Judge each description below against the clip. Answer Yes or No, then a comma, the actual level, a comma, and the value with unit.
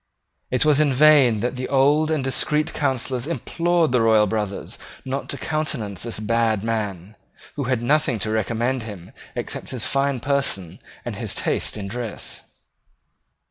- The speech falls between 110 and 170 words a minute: Yes, average, 150 wpm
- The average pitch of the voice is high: No, low, 125 Hz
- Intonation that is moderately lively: Yes, average, 4.5 semitones